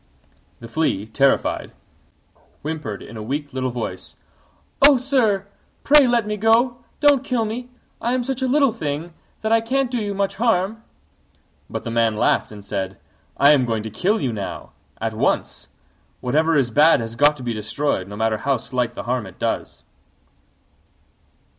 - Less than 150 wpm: No, average, 170 wpm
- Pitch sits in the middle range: Yes, medium, 150 Hz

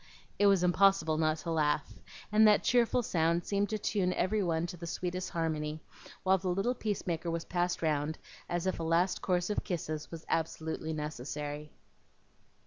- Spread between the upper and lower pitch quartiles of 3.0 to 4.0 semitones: Yes, average, 3.3 semitones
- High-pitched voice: No, medium, 170 Hz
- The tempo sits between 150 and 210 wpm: Yes, average, 170 wpm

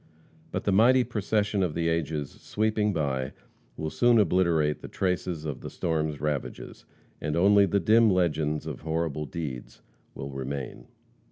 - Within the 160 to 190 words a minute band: No, average, 150 wpm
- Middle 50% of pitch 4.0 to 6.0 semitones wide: Yes, average, 5.0 semitones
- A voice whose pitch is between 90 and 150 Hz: No, very low, 80 Hz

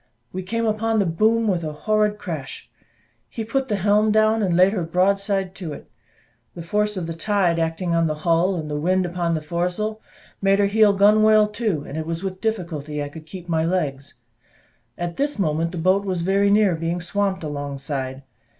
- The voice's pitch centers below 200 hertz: Yes, medium, 185 Hz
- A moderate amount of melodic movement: Yes, average, 4.2 semitones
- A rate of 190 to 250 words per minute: Yes, average, 195 wpm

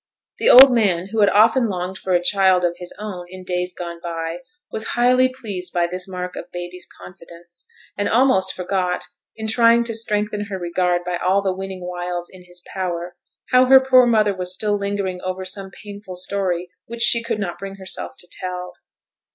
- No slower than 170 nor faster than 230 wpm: Yes, average, 190 wpm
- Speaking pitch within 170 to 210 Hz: Yes, medium, 185 Hz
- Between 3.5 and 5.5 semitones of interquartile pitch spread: No, average, 2.9 semitones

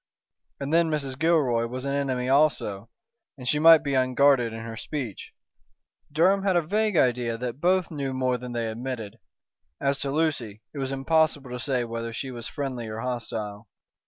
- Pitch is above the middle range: No, low, 130 Hz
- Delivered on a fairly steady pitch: No, average, 4.1 semitones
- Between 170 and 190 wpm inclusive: Yes, average, 180 wpm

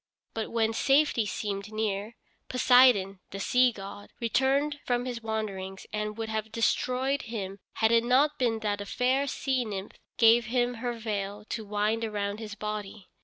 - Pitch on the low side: No, high, 220 Hz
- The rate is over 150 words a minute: Yes, average, 165 wpm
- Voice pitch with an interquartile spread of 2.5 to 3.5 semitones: Yes, average, 3.1 semitones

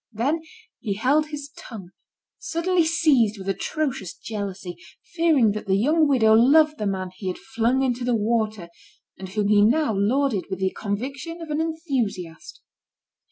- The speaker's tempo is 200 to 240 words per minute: No, average, 160 wpm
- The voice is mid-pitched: No, high, 230 Hz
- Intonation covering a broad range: Yes, wide, 6.8 semitones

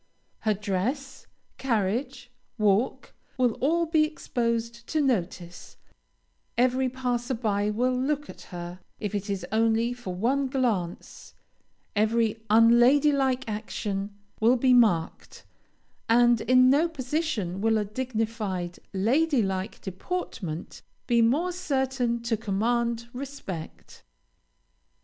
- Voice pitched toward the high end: Yes, high, 235 Hz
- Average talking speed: No, slow, 115 wpm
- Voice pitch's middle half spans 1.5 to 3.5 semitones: No, average, 3.9 semitones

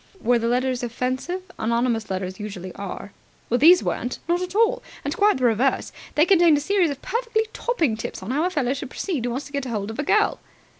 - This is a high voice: Yes, very high, 260 Hz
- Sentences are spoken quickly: Yes, fast, 215 wpm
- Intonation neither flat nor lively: No, wide, 7.1 semitones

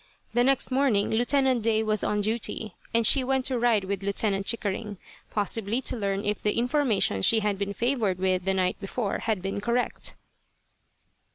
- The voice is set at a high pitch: Yes, high, 215 Hz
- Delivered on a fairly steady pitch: No, average, 3.4 semitones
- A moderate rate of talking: Yes, average, 175 wpm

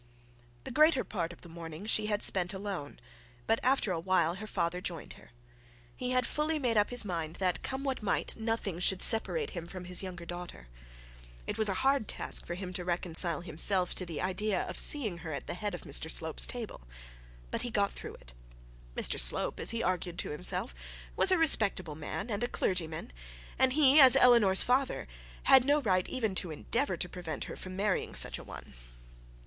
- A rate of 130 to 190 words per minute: No, average, 200 wpm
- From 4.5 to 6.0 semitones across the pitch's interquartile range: Yes, wide, 5.4 semitones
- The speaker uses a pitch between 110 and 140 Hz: No, high, 190 Hz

